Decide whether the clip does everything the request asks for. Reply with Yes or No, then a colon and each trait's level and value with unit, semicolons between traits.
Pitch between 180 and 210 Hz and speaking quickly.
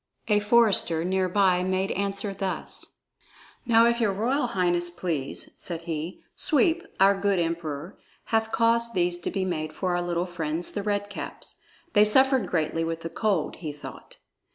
No: medium, 185 Hz; average, 165 wpm